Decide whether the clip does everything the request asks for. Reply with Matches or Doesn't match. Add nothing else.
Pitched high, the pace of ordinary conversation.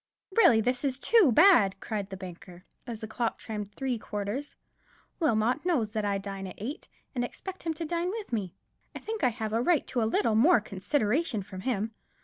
Doesn't match